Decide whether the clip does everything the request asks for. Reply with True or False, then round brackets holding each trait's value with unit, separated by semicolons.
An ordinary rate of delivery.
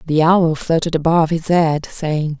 True (175 wpm)